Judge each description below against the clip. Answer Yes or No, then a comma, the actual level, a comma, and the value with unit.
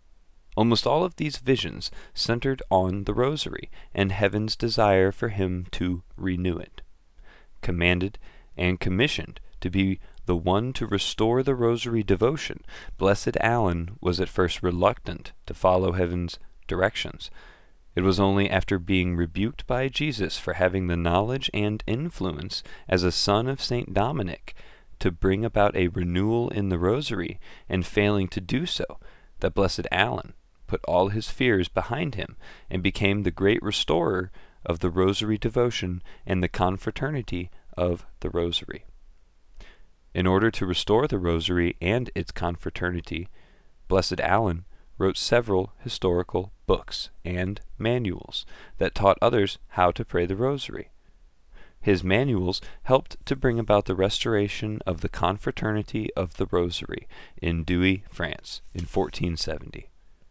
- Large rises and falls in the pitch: No, average, 3.4 semitones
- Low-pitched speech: Yes, very low, 95 Hz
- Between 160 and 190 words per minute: No, average, 140 wpm